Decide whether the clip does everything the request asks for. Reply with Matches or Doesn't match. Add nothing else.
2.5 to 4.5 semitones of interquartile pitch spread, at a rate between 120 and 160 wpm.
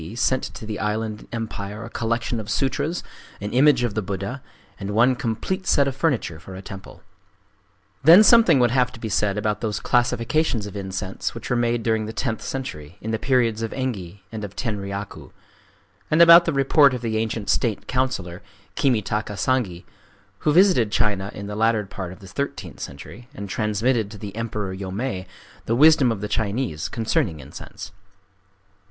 Doesn't match